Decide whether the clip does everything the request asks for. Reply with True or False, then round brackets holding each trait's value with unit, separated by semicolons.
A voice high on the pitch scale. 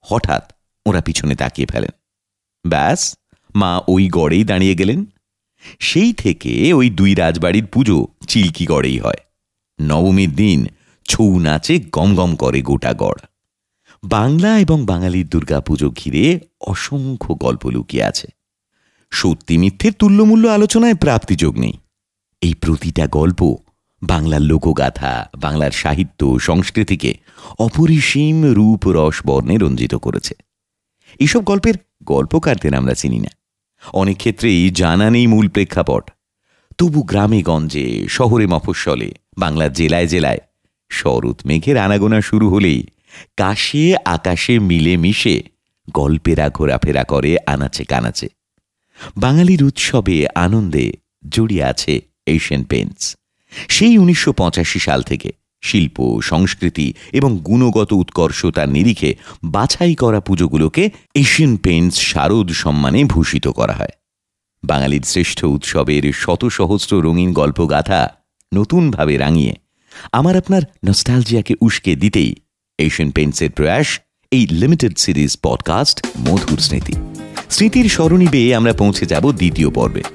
False (90 Hz)